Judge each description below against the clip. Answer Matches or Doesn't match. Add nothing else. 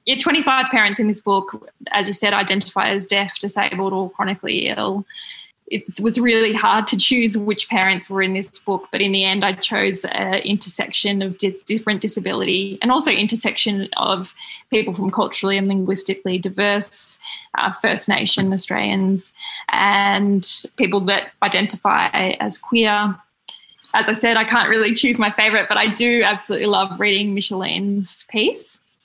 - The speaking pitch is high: Matches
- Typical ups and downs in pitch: Doesn't match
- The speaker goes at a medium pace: Matches